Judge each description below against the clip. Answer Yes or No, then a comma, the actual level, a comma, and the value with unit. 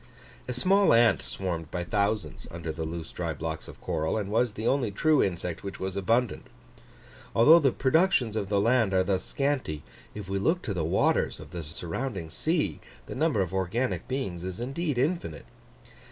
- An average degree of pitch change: No, wide, 6.8 semitones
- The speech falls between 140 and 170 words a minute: No, average, 180 wpm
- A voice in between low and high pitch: No, low, 100 Hz